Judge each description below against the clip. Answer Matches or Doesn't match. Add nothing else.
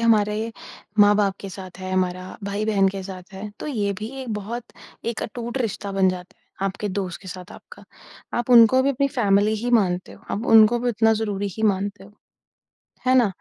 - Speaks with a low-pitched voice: Doesn't match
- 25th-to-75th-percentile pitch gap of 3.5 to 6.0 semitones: Doesn't match